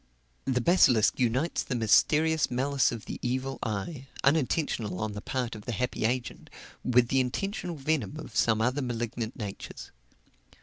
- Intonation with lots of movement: No, average, 3.7 semitones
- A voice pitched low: Yes, low, 125 Hz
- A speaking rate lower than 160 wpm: Yes, average, 150 wpm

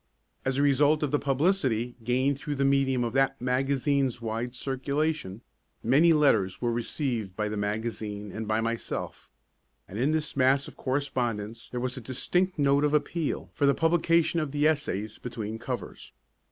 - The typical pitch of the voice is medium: No, low, 130 Hz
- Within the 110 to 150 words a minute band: No, average, 165 wpm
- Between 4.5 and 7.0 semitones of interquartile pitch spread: No, average, 4.0 semitones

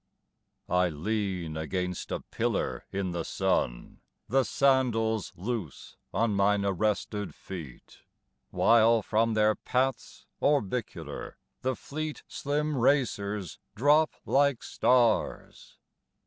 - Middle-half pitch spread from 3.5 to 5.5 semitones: Yes, average, 5.2 semitones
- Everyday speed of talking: No, slow, 100 wpm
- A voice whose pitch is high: No, low, 110 Hz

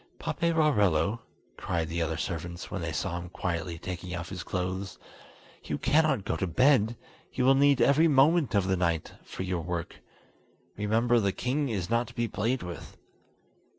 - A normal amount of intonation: No, wide, 6.5 semitones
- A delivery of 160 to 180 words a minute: Yes, average, 170 wpm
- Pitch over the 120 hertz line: No, very low, 95 Hz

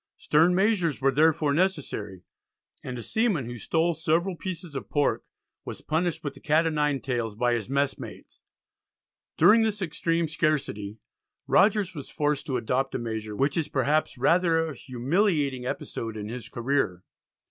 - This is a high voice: No, medium, 145 Hz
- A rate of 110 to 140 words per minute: No, average, 160 wpm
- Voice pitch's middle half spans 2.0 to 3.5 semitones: No, average, 5.1 semitones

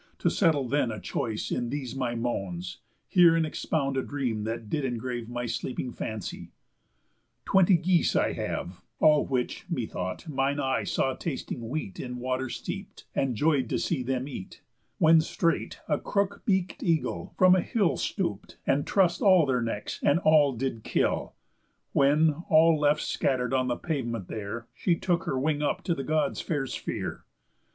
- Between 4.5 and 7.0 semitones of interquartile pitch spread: Yes, average, 4.9 semitones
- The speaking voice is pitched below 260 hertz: Yes, low, 135 Hz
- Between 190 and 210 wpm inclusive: No, average, 170 wpm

